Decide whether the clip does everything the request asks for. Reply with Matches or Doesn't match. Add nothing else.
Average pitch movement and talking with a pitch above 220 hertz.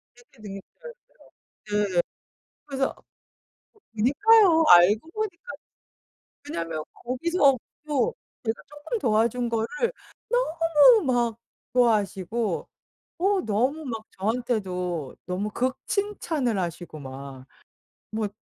Doesn't match